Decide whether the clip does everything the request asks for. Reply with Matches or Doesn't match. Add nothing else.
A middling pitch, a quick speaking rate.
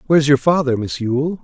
Matches